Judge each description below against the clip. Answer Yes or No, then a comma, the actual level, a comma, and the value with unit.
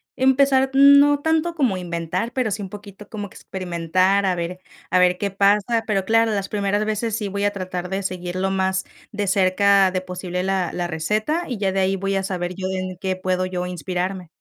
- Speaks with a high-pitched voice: Yes, high, 195 Hz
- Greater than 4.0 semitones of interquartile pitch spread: No, narrow, 2.4 semitones